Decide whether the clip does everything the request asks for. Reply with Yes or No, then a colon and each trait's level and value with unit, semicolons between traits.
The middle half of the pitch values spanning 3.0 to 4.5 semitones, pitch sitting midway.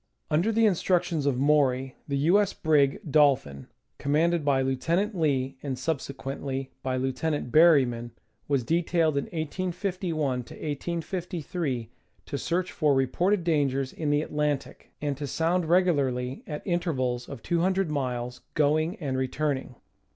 Yes: average, 4.2 semitones; medium, 150 Hz